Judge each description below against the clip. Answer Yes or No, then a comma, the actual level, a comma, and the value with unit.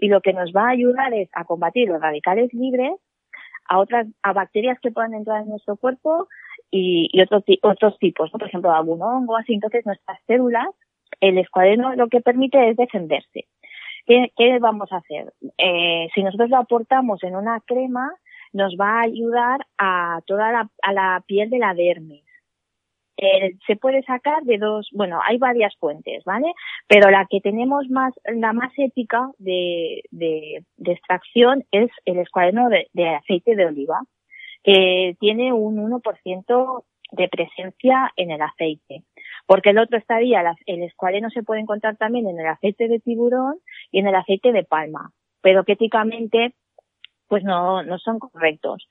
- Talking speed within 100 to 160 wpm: No, average, 170 wpm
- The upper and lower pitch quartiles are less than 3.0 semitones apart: No, average, 4.8 semitones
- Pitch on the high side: Yes, high, 215 Hz